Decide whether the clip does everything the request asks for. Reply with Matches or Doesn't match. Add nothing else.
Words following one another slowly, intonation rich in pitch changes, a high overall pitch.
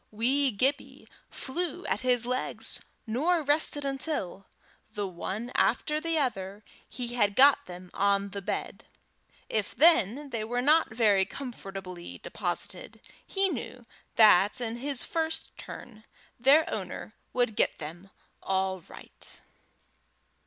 Matches